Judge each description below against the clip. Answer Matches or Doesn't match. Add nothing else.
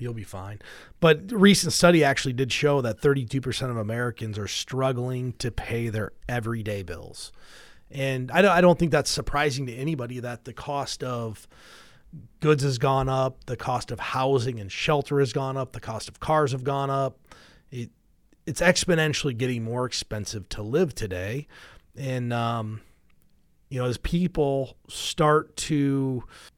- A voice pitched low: Matches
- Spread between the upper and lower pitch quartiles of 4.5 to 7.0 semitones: Doesn't match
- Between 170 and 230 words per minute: Doesn't match